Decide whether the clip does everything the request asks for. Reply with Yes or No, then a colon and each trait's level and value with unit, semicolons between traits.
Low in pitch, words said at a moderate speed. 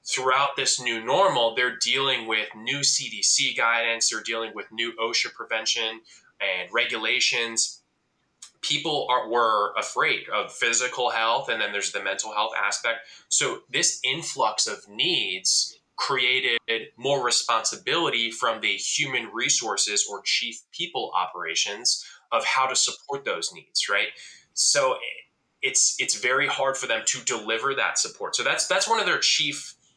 Yes: low, 125 Hz; average, 145 wpm